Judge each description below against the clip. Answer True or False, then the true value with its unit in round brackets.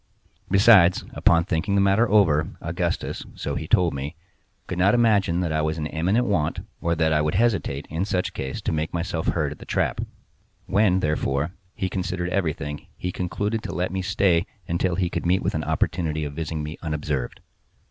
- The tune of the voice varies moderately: True (3.5 semitones)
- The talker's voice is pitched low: True (85 Hz)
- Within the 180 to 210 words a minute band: True (190 wpm)